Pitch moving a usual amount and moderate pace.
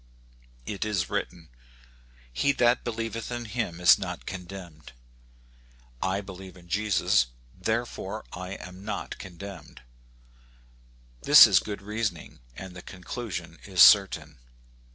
No: average, 3.4 semitones; slow, 120 wpm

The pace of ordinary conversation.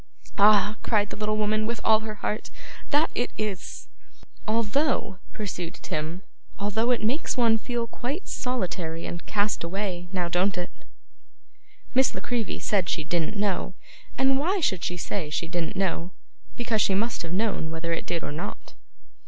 Yes: average, 165 wpm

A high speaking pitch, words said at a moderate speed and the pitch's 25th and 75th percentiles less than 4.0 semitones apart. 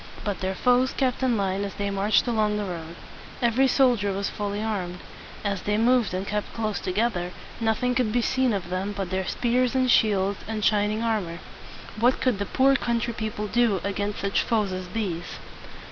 Yes: high, 210 Hz; average, 190 wpm; average, 3.3 semitones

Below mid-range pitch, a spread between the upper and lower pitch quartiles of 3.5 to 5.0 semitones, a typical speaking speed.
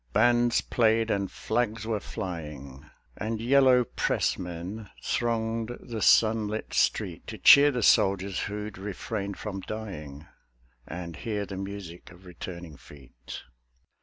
No: low, 105 Hz; average, 4.1 semitones; slow, 120 wpm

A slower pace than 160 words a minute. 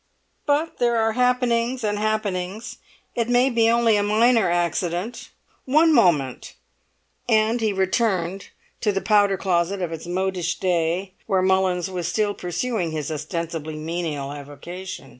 Yes: average, 140 wpm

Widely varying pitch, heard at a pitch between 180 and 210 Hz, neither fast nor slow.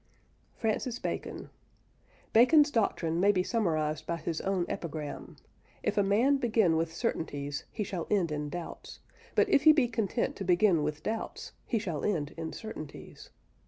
Yes: wide, 5.7 semitones; medium, 185 Hz; average, 160 wpm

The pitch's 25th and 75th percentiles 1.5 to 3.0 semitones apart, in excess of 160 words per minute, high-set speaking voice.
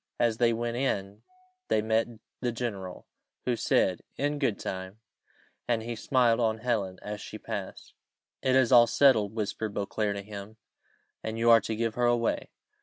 No: narrow, 2.4 semitones; average, 170 wpm; low, 115 Hz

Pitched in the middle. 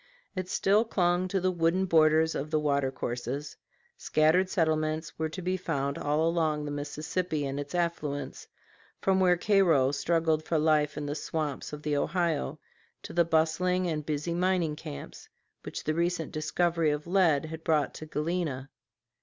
Yes: medium, 160 Hz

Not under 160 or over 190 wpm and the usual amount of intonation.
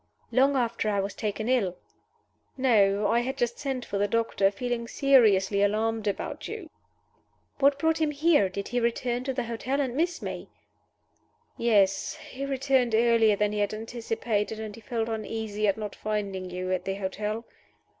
Yes: average, 170 wpm; average, 3.7 semitones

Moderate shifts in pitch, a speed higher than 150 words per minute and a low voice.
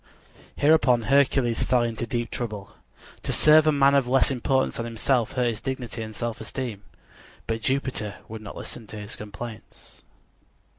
Yes: average, 3.1 semitones; average, 165 wpm; low, 120 Hz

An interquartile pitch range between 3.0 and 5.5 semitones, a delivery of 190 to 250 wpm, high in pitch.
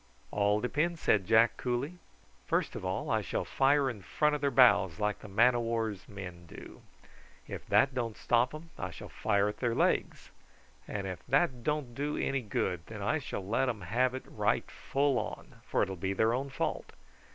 No: average, 5.0 semitones; average, 195 wpm; low, 120 Hz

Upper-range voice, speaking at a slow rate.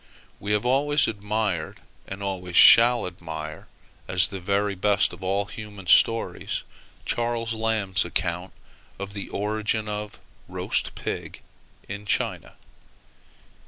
No: low, 100 Hz; slow, 120 wpm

